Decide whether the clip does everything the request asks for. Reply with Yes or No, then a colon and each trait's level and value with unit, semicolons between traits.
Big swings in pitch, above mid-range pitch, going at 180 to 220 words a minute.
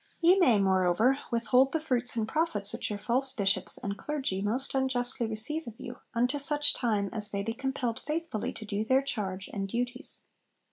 No: average, 4.6 semitones; high, 240 Hz; average, 185 wpm